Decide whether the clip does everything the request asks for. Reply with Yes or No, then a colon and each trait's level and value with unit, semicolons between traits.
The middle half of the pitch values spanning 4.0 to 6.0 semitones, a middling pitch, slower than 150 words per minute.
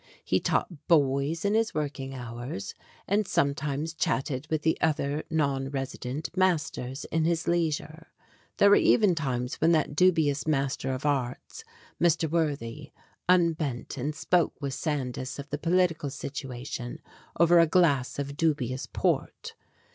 No: average, 3.5 semitones; medium, 150 Hz; average, 140 wpm